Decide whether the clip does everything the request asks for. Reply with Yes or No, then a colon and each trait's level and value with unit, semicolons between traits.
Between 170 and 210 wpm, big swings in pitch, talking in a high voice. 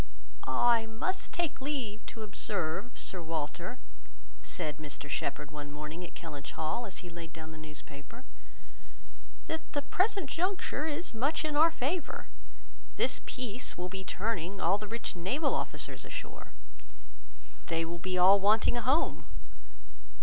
No: average, 145 wpm; wide, 8.8 semitones; high, 205 Hz